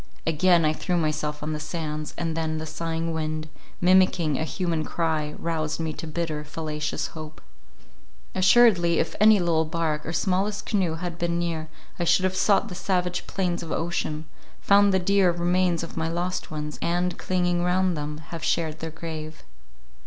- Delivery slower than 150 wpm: No, average, 175 wpm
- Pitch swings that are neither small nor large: No, narrow, 2.3 semitones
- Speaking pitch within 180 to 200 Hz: No, medium, 165 Hz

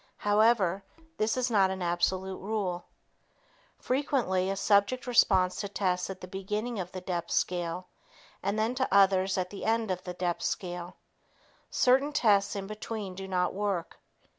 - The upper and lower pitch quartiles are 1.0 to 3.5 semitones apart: Yes, average, 2.9 semitones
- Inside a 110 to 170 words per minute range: Yes, average, 160 wpm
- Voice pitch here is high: Yes, high, 195 Hz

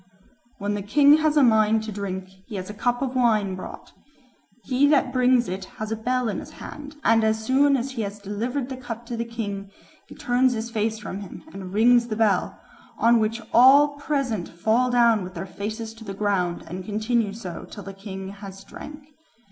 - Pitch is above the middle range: Yes, high, 220 Hz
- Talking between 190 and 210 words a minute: Yes, fast, 205 wpm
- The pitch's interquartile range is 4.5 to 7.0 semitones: No, average, 3.5 semitones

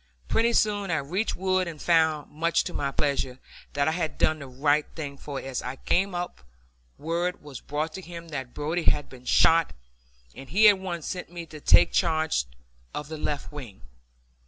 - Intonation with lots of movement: No, average, 3.6 semitones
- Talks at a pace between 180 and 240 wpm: Yes, average, 190 wpm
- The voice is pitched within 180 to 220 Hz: No, medium, 155 Hz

